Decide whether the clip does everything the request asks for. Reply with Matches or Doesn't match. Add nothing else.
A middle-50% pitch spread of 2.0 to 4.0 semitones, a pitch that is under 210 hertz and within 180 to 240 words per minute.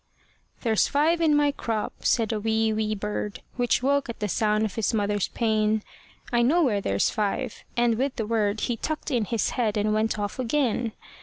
Doesn't match